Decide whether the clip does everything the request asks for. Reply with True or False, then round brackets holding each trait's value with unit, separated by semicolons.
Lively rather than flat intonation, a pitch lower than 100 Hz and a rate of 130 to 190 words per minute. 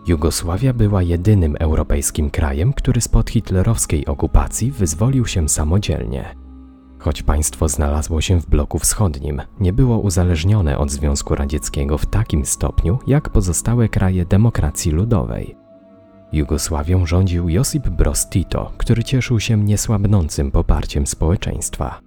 False (5.8 semitones; 90 Hz; 115 wpm)